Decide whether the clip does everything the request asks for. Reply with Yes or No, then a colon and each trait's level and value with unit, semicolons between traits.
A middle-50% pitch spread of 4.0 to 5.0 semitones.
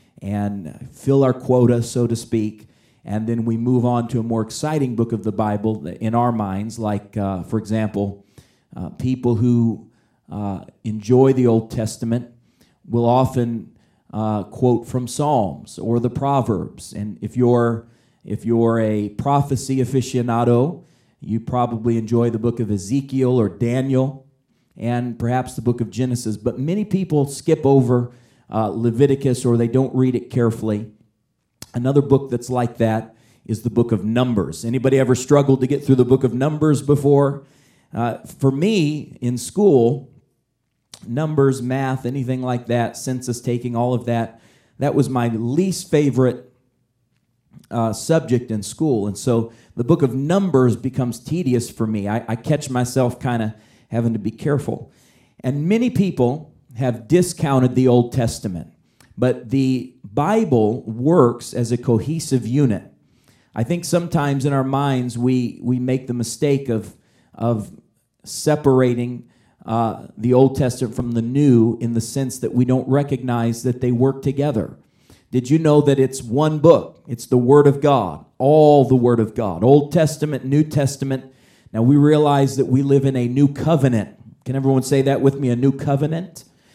No: average, 2.8 semitones